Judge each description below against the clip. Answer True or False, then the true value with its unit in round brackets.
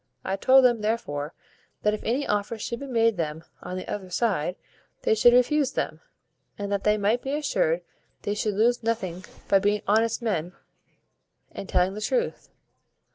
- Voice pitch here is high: True (210 Hz)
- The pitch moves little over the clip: False (3.9 semitones)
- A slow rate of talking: False (175 wpm)